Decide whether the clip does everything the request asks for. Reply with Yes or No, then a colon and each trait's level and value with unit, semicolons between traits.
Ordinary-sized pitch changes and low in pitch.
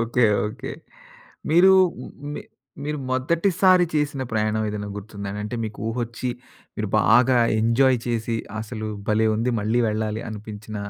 Yes: average, 3.2 semitones; low, 115 Hz